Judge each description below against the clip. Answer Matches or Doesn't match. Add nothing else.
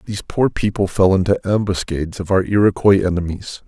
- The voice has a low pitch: Matches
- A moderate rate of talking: Matches